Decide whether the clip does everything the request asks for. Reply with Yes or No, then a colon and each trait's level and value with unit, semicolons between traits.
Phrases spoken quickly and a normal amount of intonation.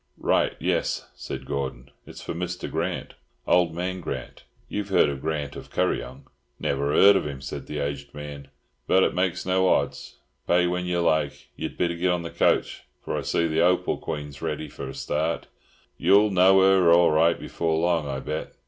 No: average, 185 wpm; average, 3.9 semitones